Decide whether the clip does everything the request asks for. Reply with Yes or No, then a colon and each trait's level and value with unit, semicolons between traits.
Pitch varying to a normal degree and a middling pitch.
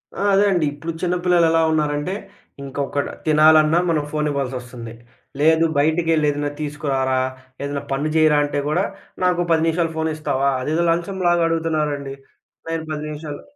No: narrow, 2.3 semitones; medium, 155 Hz